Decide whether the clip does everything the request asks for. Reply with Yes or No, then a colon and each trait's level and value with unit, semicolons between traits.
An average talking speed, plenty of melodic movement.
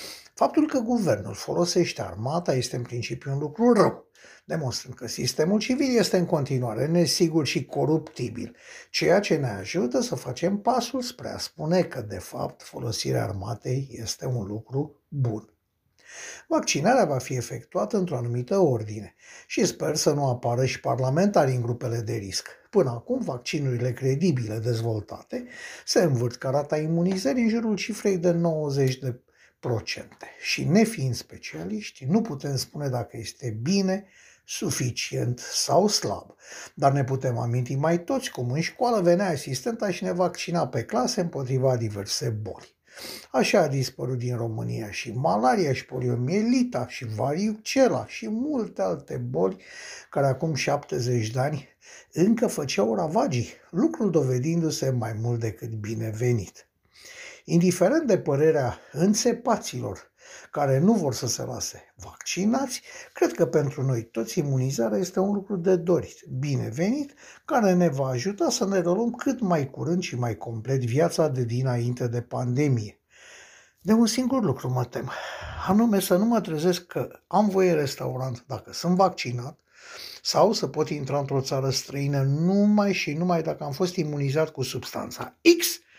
Yes: average, 145 wpm; wide, 7.3 semitones